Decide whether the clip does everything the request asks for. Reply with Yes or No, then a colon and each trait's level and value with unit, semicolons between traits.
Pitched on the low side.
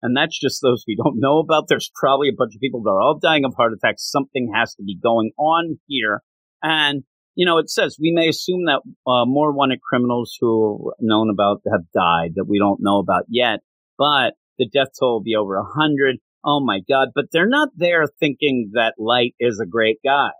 Yes: low, 125 Hz